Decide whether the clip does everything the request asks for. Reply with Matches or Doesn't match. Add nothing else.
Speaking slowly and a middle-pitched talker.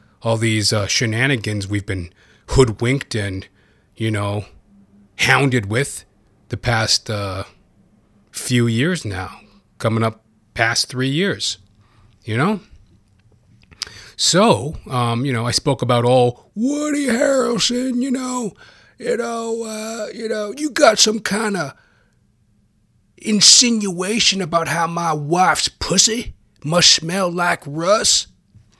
Doesn't match